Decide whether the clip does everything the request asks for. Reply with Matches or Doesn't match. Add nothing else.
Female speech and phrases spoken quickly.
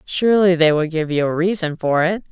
Matches